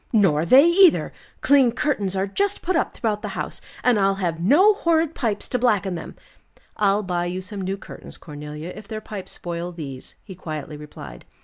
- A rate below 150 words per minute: No, average, 190 wpm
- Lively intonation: Yes, wide, 6.3 semitones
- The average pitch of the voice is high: Yes, high, 195 Hz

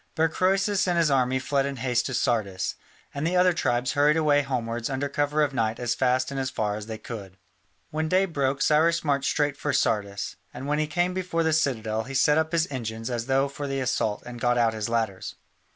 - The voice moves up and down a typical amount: Yes, average, 4.6 semitones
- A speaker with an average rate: No, fast, 225 wpm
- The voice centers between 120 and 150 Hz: Yes, low, 135 Hz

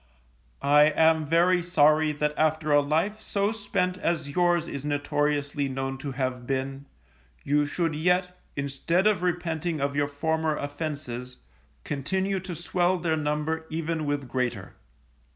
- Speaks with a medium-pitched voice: Yes, medium, 155 Hz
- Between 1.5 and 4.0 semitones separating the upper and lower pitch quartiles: Yes, average, 3.3 semitones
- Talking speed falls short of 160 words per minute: Yes, average, 140 wpm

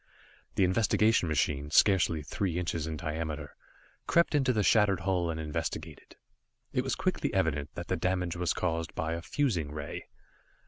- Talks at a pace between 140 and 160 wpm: Yes, average, 155 wpm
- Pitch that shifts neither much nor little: Yes, average, 3.3 semitones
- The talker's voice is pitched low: Yes, very low, 85 Hz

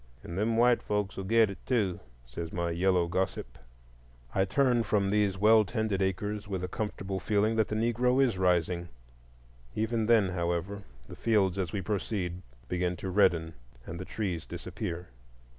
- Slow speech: No, average, 165 wpm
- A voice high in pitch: No, very low, 95 Hz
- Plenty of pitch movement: No, average, 3.3 semitones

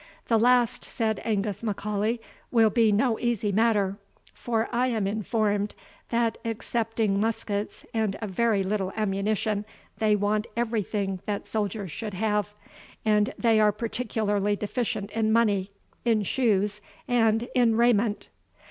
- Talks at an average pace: No, slow, 130 wpm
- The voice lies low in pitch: No, high, 215 Hz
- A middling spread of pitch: No, narrow, 1.9 semitones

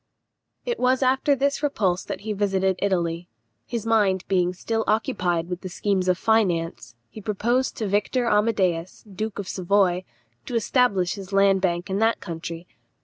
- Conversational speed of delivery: Yes, average, 155 wpm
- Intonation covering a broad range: No, average, 3.6 semitones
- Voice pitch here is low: No, high, 195 Hz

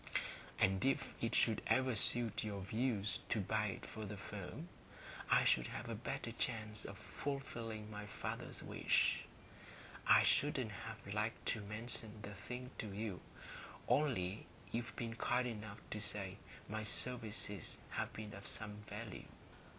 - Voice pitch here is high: No, low, 110 Hz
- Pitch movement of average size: No, narrow, 2.3 semitones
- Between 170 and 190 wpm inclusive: No, average, 150 wpm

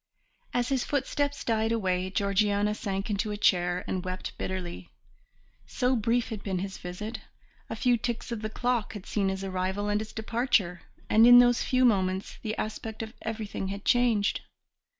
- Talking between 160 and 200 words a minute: Yes, average, 170 wpm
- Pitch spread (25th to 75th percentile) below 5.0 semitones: Yes, average, 3.4 semitones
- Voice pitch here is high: Yes, high, 210 Hz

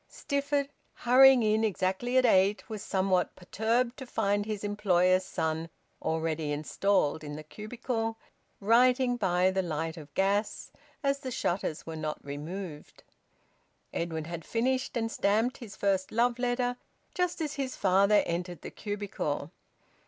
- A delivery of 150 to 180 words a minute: No, average, 140 wpm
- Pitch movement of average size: No, wide, 5.8 semitones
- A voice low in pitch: No, high, 200 Hz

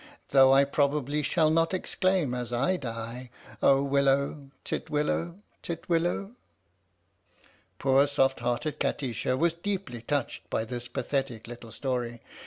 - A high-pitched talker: No, medium, 140 Hz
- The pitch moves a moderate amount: Yes, average, 4.0 semitones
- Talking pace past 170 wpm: No, slow, 135 wpm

